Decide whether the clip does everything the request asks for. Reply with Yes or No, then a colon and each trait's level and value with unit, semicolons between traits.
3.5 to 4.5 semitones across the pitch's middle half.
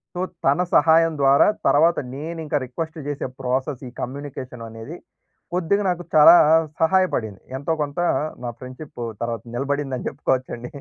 Yes: average, 4.1 semitones